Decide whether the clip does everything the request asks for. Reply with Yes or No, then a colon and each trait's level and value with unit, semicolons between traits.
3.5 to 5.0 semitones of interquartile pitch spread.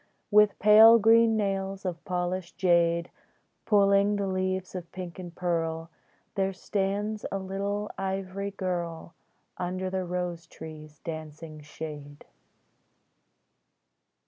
No: average, 2.8 semitones